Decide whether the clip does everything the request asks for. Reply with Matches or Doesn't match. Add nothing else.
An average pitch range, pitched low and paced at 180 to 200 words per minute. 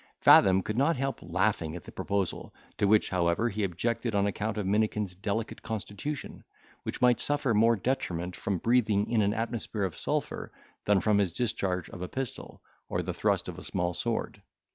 Matches